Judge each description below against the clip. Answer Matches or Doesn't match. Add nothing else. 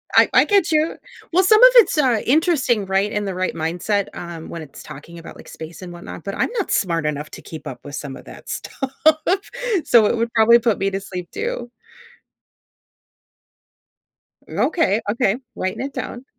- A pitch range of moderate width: Doesn't match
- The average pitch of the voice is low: Doesn't match